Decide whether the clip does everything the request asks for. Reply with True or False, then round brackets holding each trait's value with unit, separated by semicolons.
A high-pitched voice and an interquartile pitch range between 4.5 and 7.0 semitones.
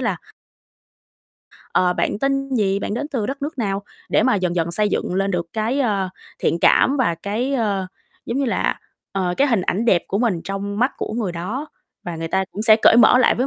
True (210 Hz; 4.8 semitones)